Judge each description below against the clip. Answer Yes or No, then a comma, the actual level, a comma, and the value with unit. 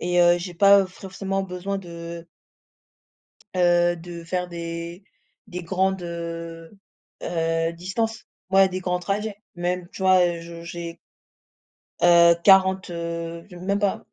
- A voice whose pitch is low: No, medium, 175 Hz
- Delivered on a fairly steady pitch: Yes, narrow, 2.0 semitones